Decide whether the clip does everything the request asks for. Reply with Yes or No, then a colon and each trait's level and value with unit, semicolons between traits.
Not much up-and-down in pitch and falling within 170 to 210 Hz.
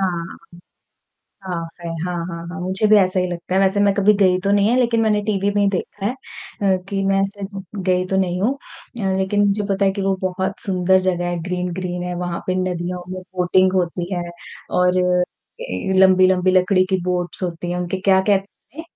Yes: narrow, 1.6 semitones; medium, 185 Hz